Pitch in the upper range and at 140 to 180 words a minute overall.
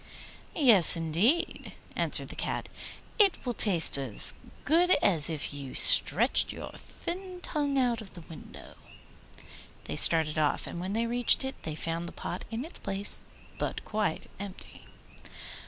Yes: high, 200 Hz; average, 155 wpm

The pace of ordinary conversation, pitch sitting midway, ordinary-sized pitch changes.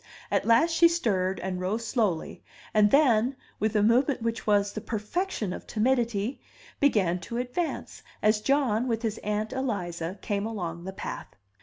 No: average, 160 wpm; high, 220 Hz; average, 3.7 semitones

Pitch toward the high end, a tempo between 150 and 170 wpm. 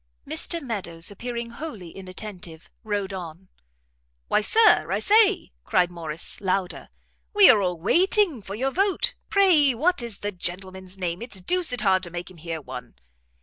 Yes: high, 195 Hz; average, 155 wpm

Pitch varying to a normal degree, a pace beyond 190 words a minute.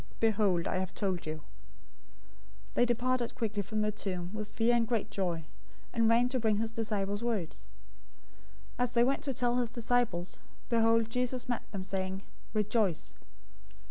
No: average, 3.5 semitones; average, 165 wpm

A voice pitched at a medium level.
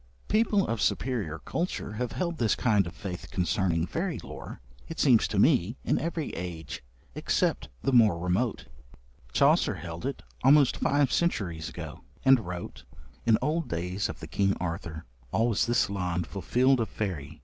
No: low, 110 Hz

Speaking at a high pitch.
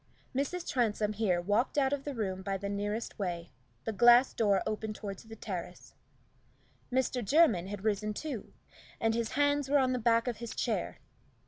Yes: high, 225 Hz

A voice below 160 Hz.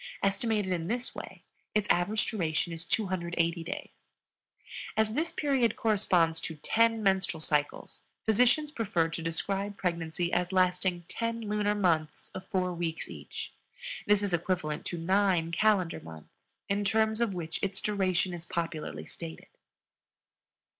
No: medium, 185 Hz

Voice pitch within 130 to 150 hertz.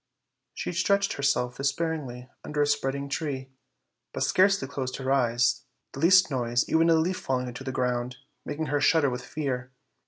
Yes: medium, 140 Hz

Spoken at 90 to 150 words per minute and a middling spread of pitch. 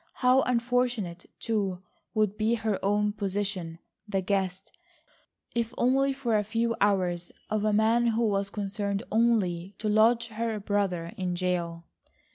Yes: slow, 135 wpm; average, 3.2 semitones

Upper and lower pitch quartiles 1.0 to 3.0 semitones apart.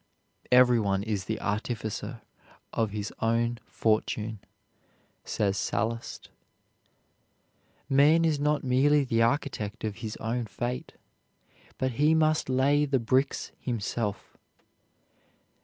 No: average, 3.9 semitones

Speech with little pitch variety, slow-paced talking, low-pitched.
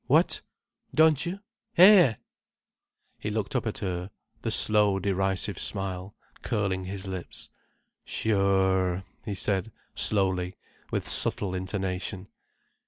Yes: narrow, 2.2 semitones; slow, 105 wpm; very low, 95 Hz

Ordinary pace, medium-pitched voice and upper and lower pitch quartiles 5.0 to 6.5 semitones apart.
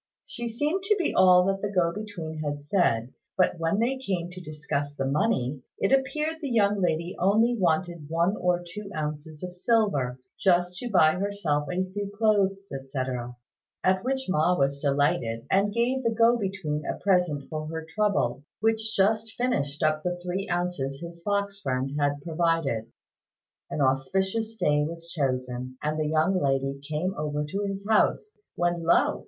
Yes: average, 170 wpm; medium, 175 Hz; wide, 5.4 semitones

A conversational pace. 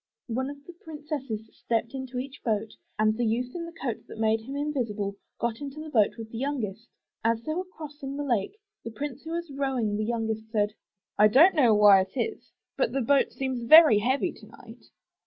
No: fast, 210 wpm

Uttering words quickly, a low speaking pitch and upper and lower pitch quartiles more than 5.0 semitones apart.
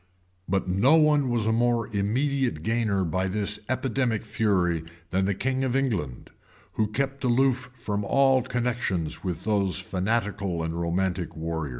No: average, 155 wpm; low, 105 Hz; wide, 5.5 semitones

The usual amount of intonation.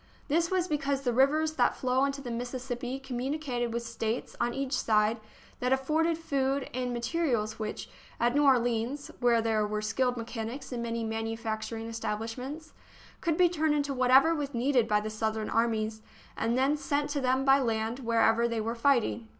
Yes: average, 3.5 semitones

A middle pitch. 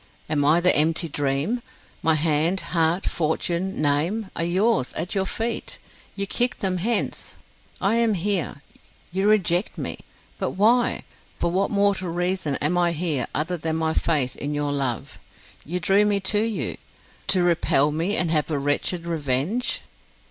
Yes: medium, 175 Hz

